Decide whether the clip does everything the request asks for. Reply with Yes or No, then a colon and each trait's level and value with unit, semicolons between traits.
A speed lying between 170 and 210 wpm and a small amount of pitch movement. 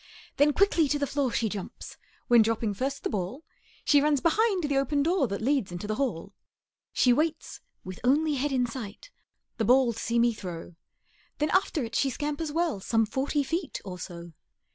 No: average, 190 wpm; average, 5.2 semitones